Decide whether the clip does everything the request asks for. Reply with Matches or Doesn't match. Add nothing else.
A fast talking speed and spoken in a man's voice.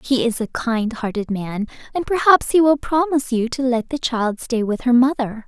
Doesn't match